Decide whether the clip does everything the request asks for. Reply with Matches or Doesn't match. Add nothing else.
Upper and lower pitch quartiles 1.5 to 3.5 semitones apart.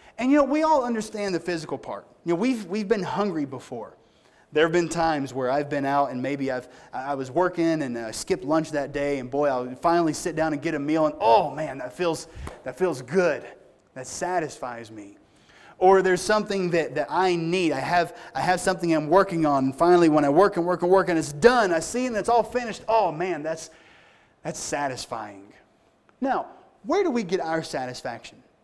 Doesn't match